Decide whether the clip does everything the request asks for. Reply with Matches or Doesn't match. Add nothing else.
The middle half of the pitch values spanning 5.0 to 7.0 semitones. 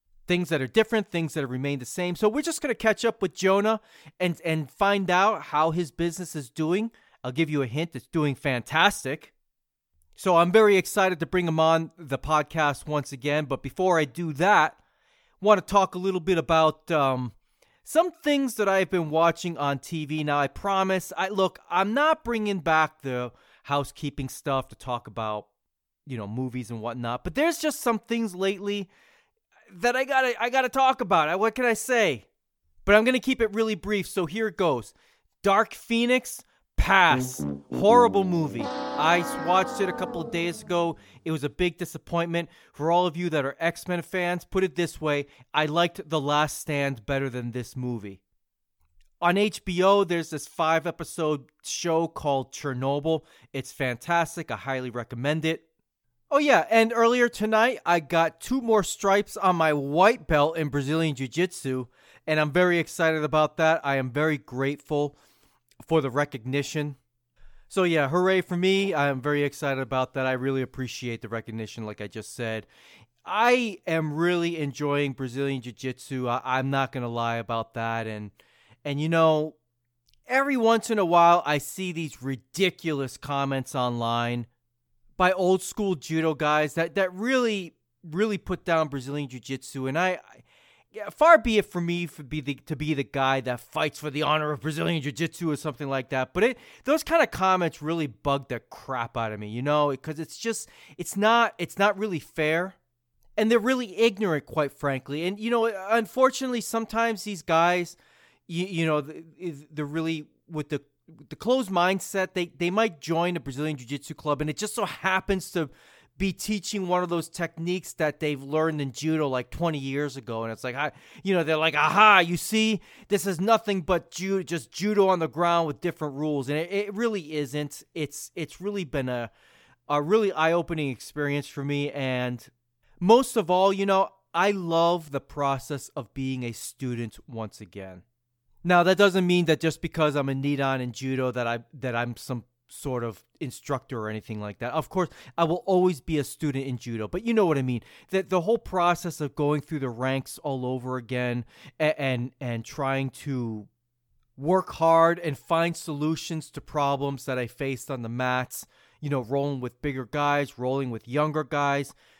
Matches